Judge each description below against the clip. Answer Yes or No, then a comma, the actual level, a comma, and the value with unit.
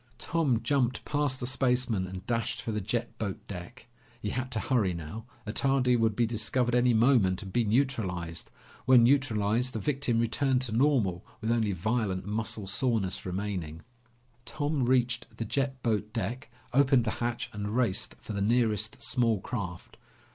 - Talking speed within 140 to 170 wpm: Yes, average, 160 wpm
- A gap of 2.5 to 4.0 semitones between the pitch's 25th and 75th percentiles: Yes, average, 3.6 semitones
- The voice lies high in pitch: No, low, 115 Hz